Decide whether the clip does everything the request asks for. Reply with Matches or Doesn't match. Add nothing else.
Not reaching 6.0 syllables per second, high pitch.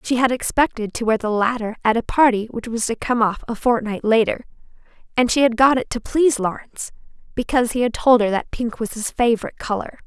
Doesn't match